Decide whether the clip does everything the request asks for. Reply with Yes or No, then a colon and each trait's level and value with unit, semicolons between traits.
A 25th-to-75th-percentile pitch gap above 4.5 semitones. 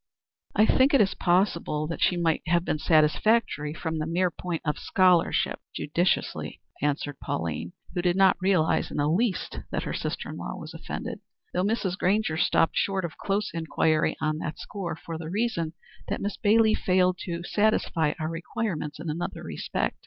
No: average, 3.7 semitones